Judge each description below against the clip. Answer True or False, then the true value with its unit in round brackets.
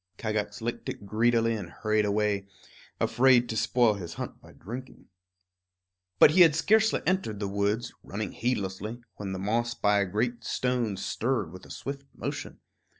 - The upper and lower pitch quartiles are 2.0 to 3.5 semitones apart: True (3.2 semitones)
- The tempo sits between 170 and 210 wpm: False (160 wpm)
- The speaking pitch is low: True (110 Hz)